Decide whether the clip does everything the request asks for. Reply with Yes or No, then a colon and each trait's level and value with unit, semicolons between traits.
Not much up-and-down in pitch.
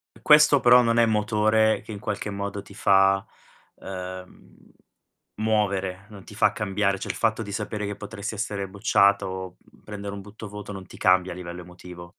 Yes: narrow, 1.9 semitones